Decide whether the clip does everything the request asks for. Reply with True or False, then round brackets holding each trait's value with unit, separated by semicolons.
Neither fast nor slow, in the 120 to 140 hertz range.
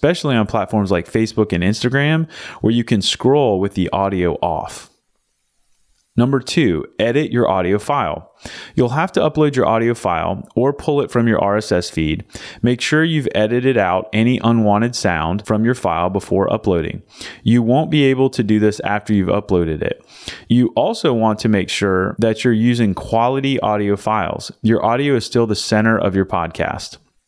False (175 wpm; 110 Hz)